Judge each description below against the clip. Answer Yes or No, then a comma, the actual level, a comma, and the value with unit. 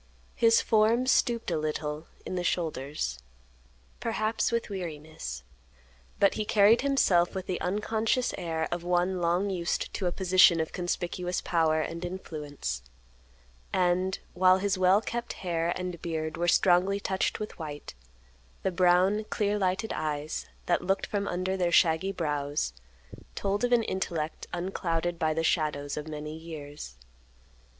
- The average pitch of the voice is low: No, medium, 175 Hz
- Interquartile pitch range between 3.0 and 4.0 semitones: Yes, average, 3.5 semitones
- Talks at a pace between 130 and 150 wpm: Yes, average, 145 wpm